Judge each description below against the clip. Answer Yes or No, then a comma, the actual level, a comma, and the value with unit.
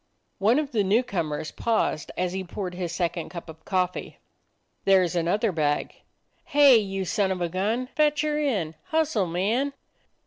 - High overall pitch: Yes, high, 195 Hz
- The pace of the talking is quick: No, average, 170 wpm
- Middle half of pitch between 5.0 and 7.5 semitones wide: Yes, wide, 5.5 semitones